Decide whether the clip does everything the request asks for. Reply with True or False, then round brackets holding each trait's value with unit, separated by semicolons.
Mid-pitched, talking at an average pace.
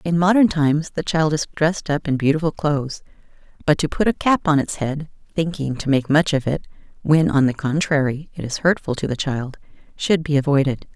False (150 Hz; 210 wpm)